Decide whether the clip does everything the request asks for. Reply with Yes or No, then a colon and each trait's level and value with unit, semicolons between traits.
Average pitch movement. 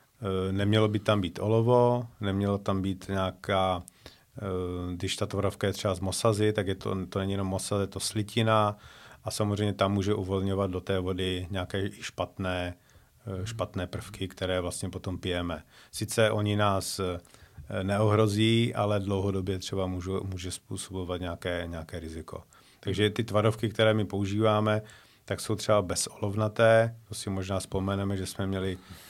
No: narrow, 2.3 semitones